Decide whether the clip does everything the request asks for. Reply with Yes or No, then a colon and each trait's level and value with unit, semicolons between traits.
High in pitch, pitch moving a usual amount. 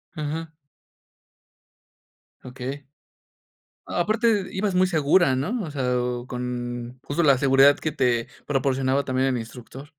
No: low, 135 Hz; average, 4.1 semitones